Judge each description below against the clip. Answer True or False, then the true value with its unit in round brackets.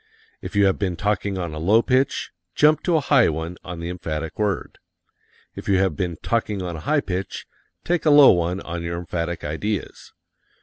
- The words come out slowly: False (200 wpm)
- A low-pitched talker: True (95 Hz)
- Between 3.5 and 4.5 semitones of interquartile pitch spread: True (4.0 semitones)